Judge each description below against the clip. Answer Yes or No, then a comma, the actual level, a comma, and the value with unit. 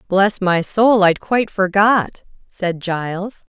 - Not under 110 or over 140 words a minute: Yes, slow, 135 wpm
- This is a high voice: Yes, high, 195 Hz